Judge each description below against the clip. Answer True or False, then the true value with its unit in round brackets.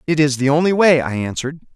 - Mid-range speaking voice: True (150 Hz)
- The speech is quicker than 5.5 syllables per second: True (6.4 syllables/s)